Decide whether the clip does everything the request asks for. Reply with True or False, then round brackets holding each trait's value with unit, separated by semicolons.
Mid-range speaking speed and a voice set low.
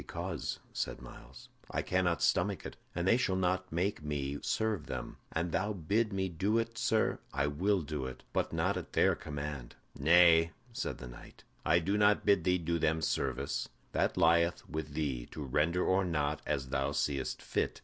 True (185 wpm; 80 Hz)